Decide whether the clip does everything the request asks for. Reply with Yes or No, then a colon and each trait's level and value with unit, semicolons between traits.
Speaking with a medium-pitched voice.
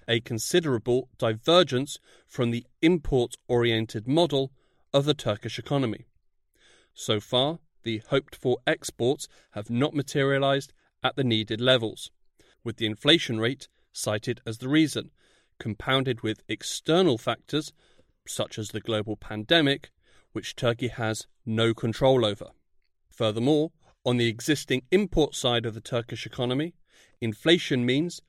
No: low, 125 Hz